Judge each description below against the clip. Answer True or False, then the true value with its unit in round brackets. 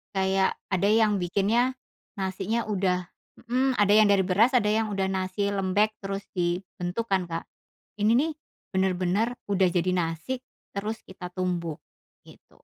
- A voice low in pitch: False (195 Hz)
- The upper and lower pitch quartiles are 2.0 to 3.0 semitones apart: True (2.7 semitones)